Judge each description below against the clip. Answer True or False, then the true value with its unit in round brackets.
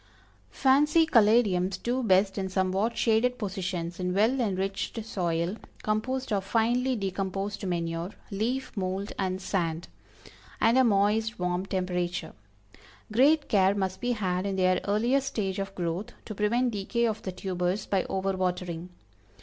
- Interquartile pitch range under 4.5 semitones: True (3.6 semitones)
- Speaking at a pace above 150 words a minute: False (140 wpm)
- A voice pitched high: True (195 Hz)